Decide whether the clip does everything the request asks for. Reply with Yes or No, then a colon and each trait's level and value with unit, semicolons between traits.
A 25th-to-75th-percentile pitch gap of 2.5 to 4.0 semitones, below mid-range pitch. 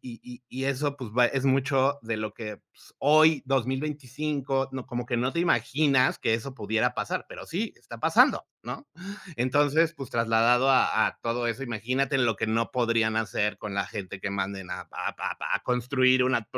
Yes: average, 3.2 semitones; low, 125 Hz